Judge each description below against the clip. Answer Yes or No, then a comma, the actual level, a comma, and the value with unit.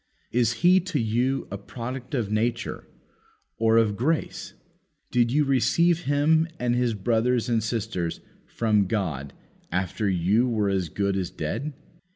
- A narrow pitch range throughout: No, average, 4.4 semitones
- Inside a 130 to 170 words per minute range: Yes, average, 145 wpm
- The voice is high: No, low, 115 Hz